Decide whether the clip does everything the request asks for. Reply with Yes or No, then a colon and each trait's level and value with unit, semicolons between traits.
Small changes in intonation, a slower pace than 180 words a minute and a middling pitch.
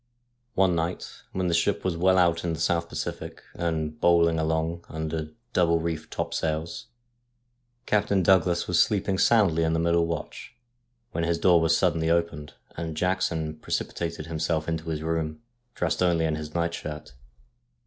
No: narrow, 1.5 semitones; average, 160 wpm; very low, 85 Hz